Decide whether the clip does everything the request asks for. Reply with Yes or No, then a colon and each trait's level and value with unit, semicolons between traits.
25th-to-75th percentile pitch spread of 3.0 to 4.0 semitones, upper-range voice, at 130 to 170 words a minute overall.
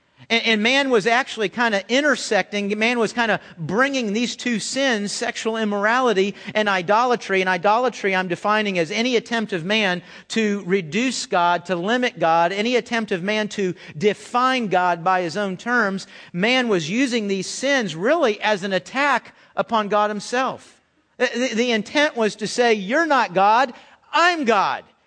Yes: average, 3.7 semitones; high, 215 Hz; average, 165 wpm